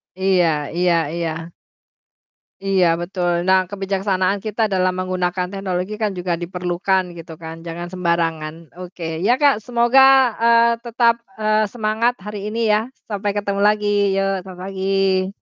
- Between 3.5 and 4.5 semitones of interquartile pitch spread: No, average, 3.0 semitones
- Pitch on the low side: No, high, 190 Hz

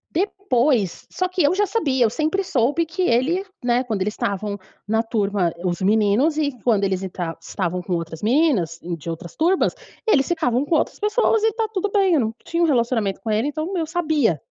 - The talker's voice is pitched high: Yes, very high, 250 Hz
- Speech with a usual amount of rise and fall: No, wide, 8.8 semitones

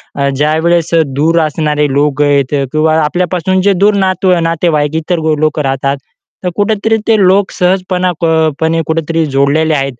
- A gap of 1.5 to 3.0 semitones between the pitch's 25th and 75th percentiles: No, average, 3.4 semitones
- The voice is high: No, medium, 160 Hz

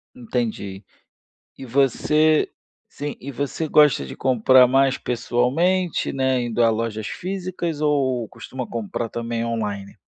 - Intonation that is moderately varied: Yes, average, 4.0 semitones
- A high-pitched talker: No, low, 125 Hz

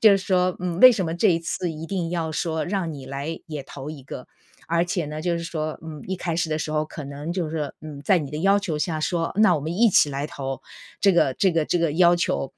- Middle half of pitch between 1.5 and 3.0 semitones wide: Yes, average, 2.7 semitones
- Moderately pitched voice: Yes, medium, 165 Hz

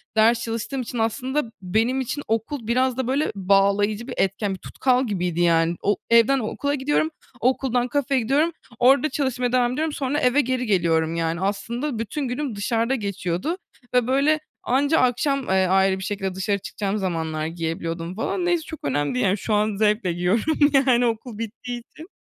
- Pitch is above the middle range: Yes, high, 230 Hz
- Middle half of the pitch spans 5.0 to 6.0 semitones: Yes, average, 5.3 semitones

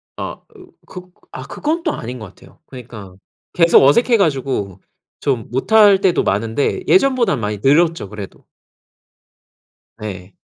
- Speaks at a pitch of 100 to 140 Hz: Yes, low, 135 Hz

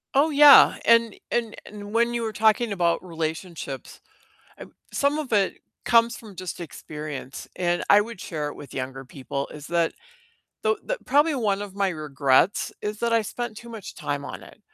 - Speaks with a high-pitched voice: Yes, high, 205 Hz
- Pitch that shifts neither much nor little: No, wide, 6.7 semitones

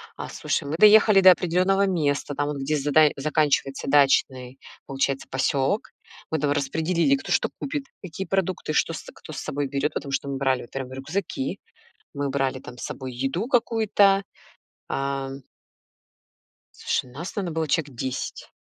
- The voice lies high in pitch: No, medium, 145 Hz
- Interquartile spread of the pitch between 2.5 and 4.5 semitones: No, average, 5.1 semitones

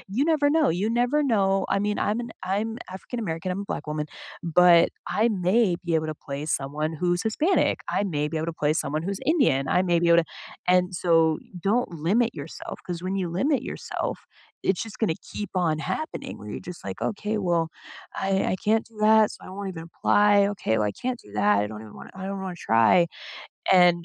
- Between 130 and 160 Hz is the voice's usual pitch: No, medium, 180 Hz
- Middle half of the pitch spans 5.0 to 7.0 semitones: Yes, wide, 5.6 semitones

